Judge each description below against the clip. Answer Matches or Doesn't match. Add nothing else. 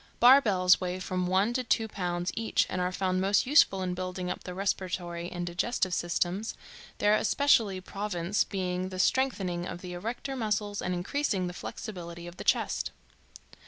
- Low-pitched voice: Doesn't match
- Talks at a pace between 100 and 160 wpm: Doesn't match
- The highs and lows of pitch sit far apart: Doesn't match